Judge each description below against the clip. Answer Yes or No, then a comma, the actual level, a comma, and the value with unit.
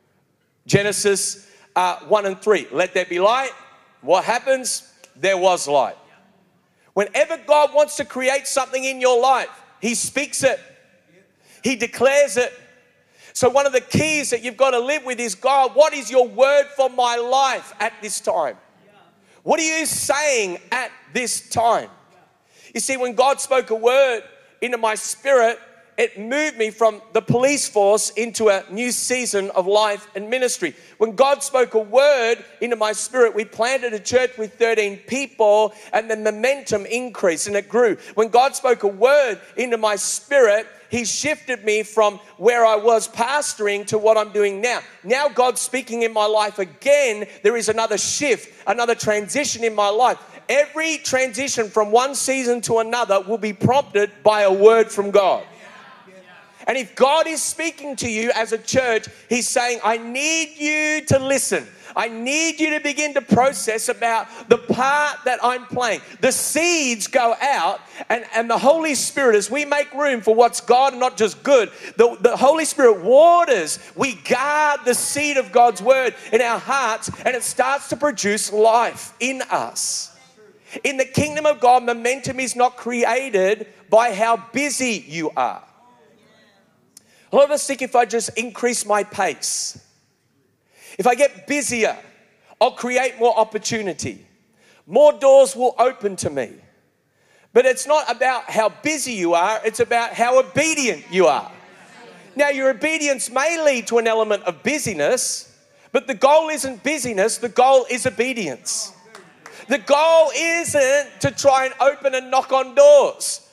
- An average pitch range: Yes, average, 4.0 semitones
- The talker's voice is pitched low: No, high, 245 Hz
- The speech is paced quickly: No, average, 165 wpm